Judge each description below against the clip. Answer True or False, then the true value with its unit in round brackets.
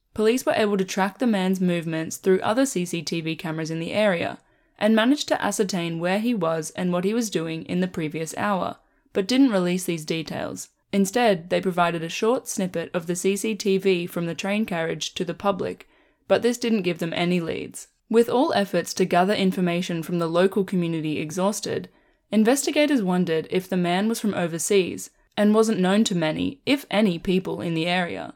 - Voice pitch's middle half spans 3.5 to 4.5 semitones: True (3.8 semitones)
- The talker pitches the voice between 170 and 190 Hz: True (185 Hz)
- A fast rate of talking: False (190 wpm)